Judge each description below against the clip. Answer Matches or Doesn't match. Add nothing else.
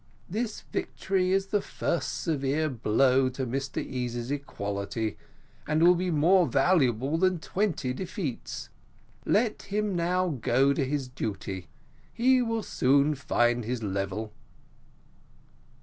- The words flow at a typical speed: Doesn't match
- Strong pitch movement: Matches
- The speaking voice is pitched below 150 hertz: Matches